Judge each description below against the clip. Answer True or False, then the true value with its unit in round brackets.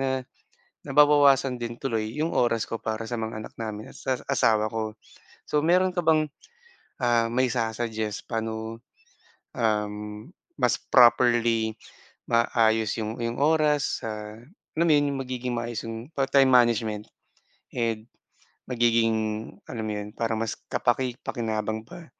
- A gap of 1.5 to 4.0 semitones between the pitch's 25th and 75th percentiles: True (2.9 semitones)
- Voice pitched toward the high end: False (115 Hz)